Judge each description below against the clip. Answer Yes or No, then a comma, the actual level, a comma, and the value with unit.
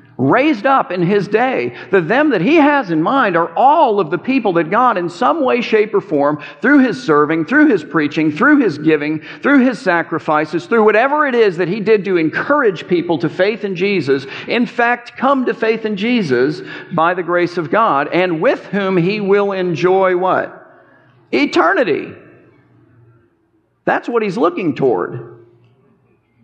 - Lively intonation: Yes, wide, 6.8 semitones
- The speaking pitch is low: No, high, 190 Hz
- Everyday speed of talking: Yes, average, 175 wpm